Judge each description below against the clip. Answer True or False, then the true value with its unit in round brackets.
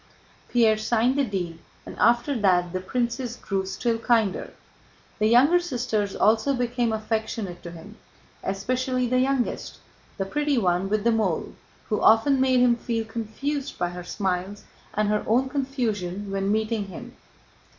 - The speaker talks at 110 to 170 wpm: True (150 wpm)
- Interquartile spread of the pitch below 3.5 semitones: False (4.1 semitones)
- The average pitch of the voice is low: False (225 Hz)